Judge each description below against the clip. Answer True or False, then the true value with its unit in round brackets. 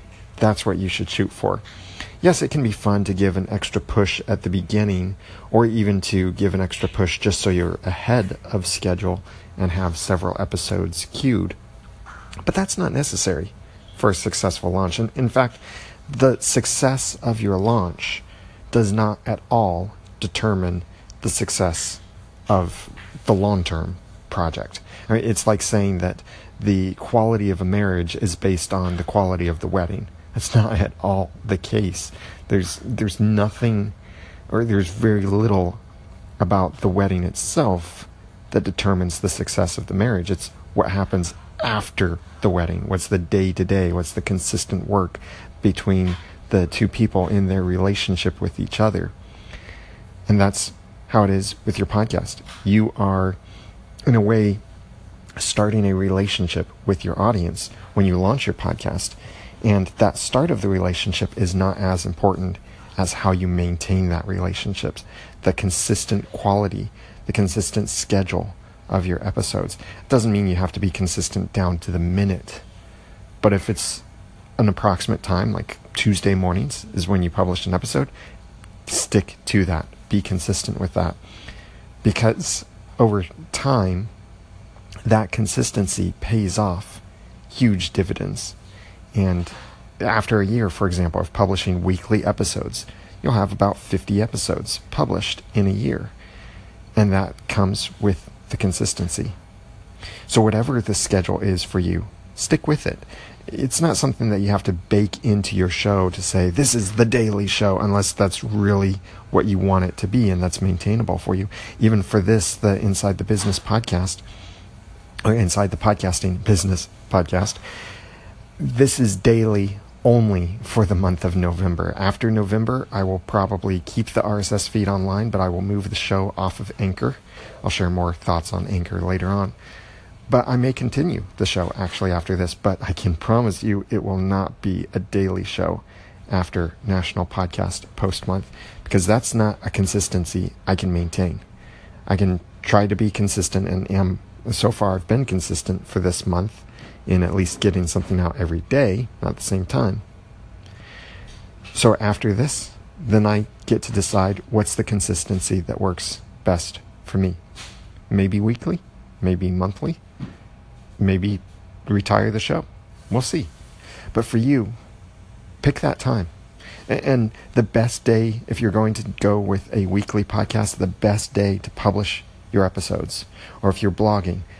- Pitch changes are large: False (2.4 semitones)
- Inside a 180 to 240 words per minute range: False (155 wpm)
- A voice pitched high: False (100 Hz)